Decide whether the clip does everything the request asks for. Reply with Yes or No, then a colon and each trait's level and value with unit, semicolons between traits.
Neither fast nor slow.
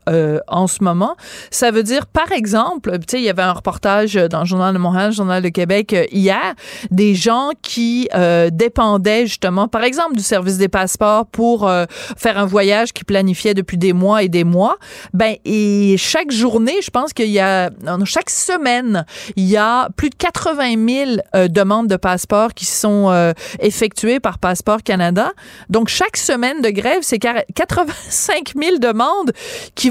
Yes: average, 180 wpm